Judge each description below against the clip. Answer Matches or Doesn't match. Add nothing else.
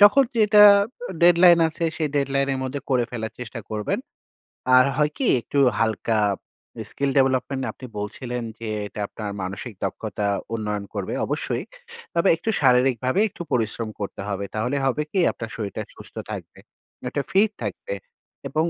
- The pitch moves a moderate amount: Doesn't match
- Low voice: Matches